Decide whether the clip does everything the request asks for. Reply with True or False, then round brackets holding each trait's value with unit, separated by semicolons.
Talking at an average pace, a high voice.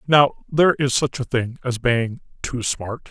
False (195 wpm; 130 Hz)